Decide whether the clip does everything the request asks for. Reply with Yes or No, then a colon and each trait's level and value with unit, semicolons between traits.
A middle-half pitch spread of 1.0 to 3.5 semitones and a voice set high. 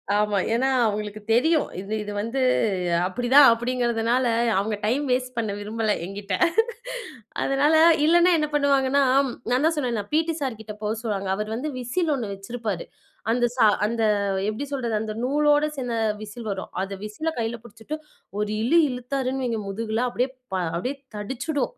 No: average, 4.2 semitones; high, 240 Hz